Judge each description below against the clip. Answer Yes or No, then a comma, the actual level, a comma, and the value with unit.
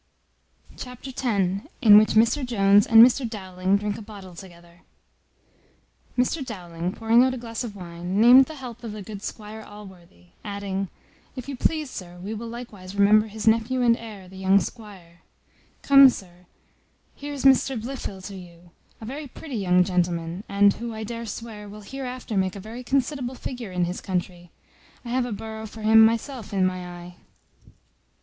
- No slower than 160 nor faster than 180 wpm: Yes, average, 175 wpm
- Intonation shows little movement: No, average, 4.3 semitones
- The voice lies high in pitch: Yes, high, 215 Hz